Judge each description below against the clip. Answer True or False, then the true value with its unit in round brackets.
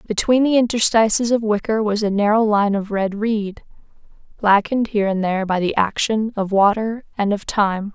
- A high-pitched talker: True (210 Hz)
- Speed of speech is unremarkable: True (180 wpm)